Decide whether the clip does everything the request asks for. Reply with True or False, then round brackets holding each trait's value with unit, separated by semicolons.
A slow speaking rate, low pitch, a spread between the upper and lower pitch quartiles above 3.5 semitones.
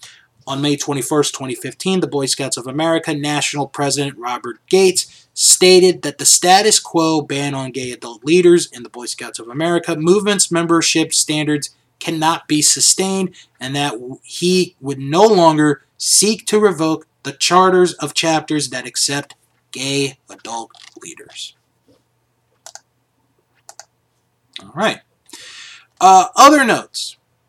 False (125 wpm; 155 Hz; 4.4 semitones)